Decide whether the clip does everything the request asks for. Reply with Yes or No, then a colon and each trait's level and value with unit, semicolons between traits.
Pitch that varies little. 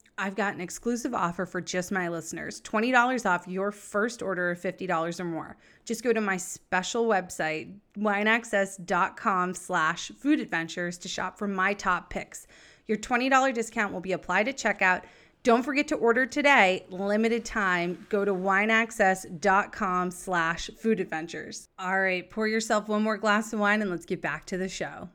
No: average, 3.5 semitones